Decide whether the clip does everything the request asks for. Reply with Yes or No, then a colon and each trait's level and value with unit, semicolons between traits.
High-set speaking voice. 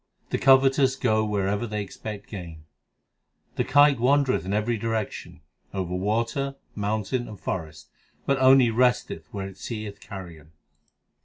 No: low, 110 Hz